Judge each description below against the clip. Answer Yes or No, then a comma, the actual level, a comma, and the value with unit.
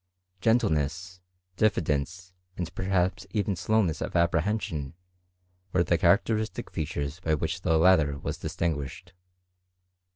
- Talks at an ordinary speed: No, slow, 105 wpm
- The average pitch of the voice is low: Yes, very low, 90 Hz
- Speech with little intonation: No, average, 3.5 semitones